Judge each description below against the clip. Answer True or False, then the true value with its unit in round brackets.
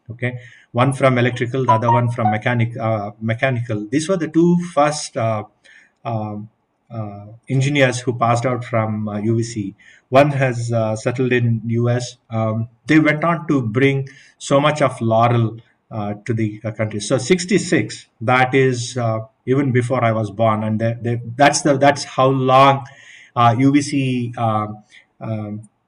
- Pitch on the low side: True (120 Hz)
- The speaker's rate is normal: True (160 wpm)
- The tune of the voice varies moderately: True (3.3 semitones)